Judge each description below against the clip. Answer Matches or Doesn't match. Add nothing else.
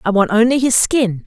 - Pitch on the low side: Doesn't match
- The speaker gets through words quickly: Matches